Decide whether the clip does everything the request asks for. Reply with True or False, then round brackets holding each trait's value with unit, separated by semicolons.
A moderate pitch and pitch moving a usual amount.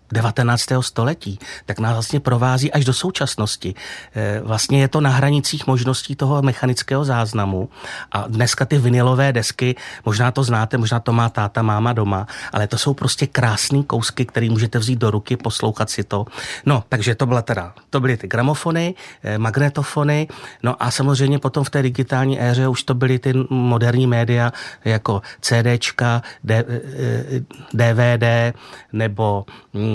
False (125 Hz; 3.0 semitones)